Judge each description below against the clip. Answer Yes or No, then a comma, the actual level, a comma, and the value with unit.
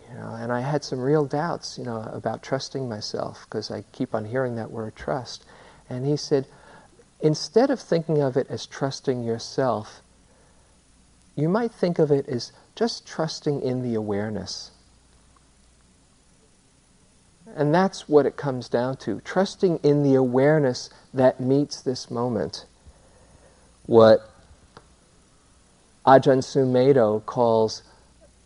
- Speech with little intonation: No, average, 4.9 semitones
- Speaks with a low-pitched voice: Yes, low, 130 Hz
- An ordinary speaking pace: No, slow, 130 wpm